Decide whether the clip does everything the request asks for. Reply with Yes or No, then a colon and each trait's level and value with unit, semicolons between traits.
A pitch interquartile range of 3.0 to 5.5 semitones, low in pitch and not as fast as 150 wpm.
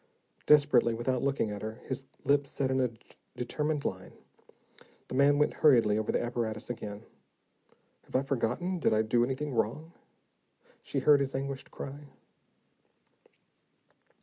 Yes: average, 3.6 semitones; low, 130 Hz; average, 140 wpm